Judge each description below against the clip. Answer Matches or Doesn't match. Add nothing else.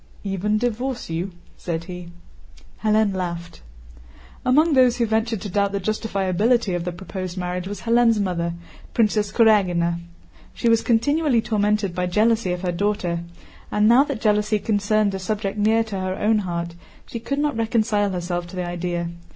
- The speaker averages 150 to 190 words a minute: Matches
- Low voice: Doesn't match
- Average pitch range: Matches